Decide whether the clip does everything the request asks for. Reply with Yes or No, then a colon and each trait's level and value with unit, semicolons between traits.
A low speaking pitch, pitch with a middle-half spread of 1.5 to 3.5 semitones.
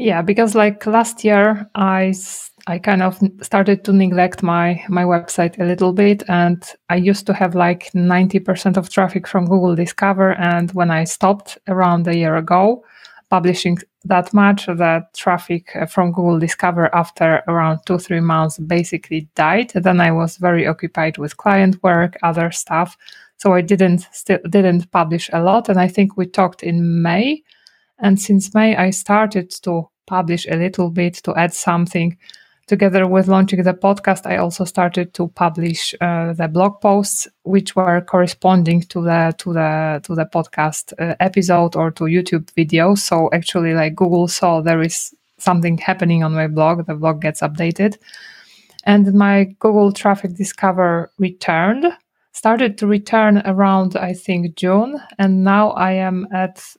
No: medium, 180 Hz; narrow, 2.5 semitones